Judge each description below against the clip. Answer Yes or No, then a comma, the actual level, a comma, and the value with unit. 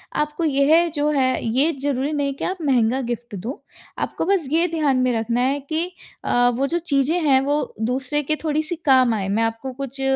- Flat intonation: No, average, 3.3 semitones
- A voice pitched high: Yes, very high, 275 Hz